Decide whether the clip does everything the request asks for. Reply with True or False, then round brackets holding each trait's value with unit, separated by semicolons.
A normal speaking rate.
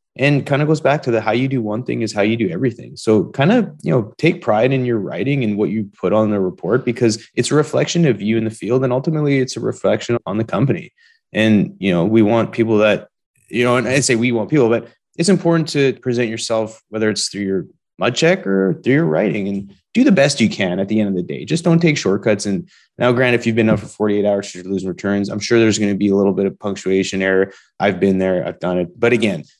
False (265 wpm)